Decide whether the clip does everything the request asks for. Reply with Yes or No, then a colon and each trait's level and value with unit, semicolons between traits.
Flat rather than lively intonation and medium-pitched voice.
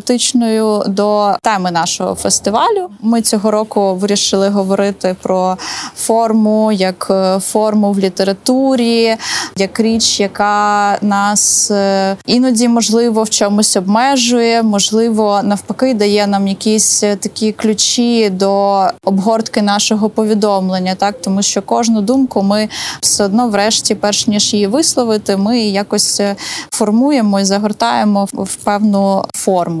No: narrow, 2.1 semitones; high, 210 Hz